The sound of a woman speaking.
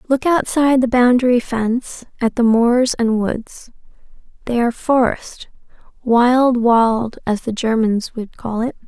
Yes: female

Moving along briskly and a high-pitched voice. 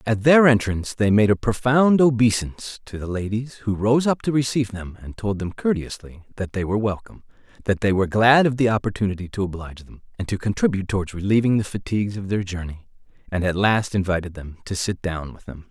No: fast, 210 wpm; low, 105 Hz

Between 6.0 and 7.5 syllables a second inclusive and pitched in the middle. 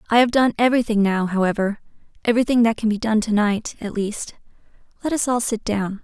No: 6.1 syllables/s; high, 220 Hz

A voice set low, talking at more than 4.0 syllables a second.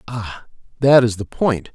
No: low, 115 Hz; 3.9 syllables/s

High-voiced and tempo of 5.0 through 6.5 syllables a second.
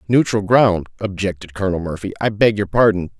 No: low, 100 Hz; 5.8 syllables/s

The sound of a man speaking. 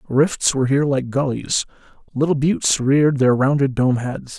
Yes: male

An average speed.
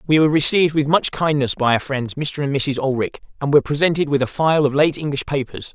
No: fast, 240 wpm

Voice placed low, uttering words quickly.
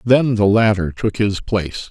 No: low, 105 Hz; average, 190 wpm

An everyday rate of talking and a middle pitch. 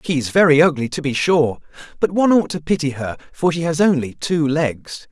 No: fast, 225 wpm; medium, 150 Hz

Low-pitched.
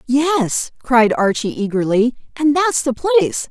No: very high, 260 Hz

